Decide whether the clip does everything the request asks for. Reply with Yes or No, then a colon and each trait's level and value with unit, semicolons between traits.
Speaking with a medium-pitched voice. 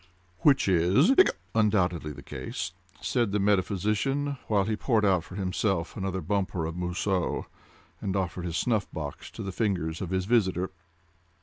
No: very low, 95 Hz